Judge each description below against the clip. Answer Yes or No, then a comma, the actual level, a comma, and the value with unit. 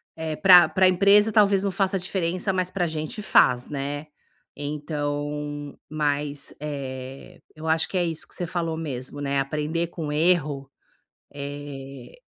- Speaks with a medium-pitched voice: Yes, medium, 150 Hz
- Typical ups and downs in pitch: Yes, average, 3.6 semitones